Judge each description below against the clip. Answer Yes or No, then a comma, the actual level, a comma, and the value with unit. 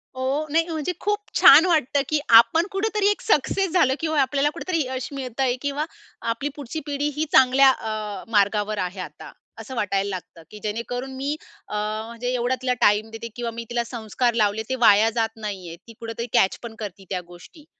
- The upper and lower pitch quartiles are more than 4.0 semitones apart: Yes, average, 5.2 semitones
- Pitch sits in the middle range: No, high, 245 Hz